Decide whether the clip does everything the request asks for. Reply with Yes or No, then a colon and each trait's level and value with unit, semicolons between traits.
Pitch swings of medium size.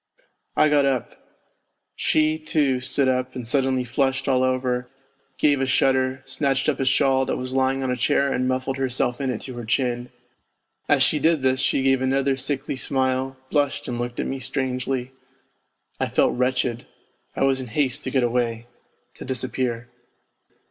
No: narrow, 1.2 semitones